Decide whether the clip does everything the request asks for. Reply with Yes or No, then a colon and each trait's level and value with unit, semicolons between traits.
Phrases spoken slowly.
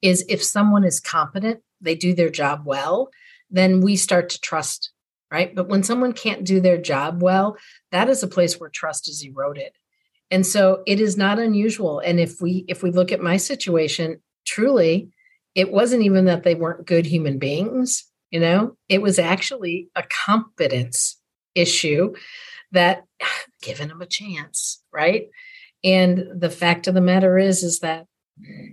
No: average, 165 wpm